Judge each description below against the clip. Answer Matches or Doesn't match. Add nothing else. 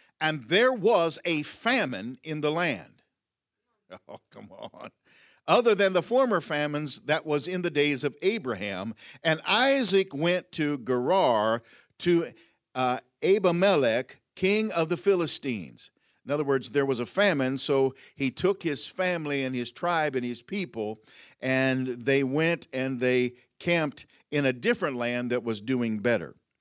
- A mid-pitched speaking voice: Matches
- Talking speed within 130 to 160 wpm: Matches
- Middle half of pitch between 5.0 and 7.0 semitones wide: Matches